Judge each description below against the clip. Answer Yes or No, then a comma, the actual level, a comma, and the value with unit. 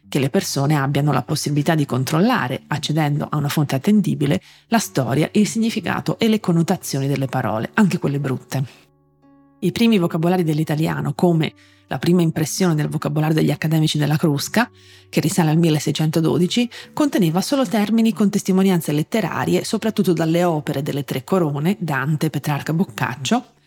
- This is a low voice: No, medium, 160 Hz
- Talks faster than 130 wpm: Yes, average, 145 wpm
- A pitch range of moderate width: Yes, average, 4.6 semitones